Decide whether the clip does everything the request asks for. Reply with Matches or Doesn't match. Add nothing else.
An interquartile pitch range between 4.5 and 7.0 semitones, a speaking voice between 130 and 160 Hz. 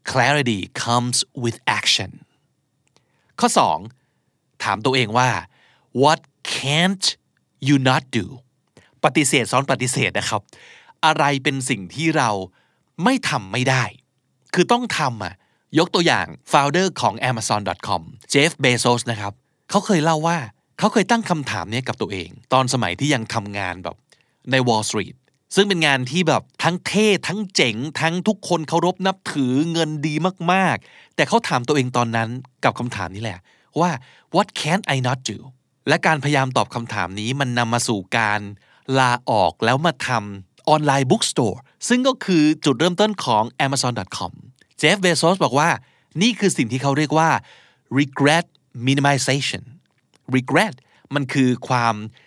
Matches